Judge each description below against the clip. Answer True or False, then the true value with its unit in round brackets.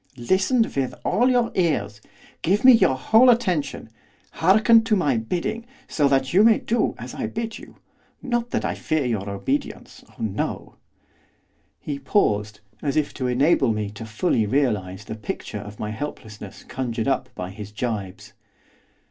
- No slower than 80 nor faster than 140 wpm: False (160 wpm)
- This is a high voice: False (135 Hz)